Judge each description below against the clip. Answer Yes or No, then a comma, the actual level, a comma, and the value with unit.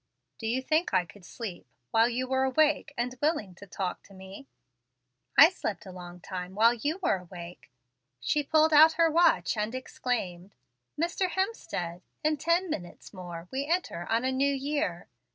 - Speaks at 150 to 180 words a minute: Yes, average, 170 wpm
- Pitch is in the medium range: No, high, 240 Hz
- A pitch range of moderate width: No, wide, 8.7 semitones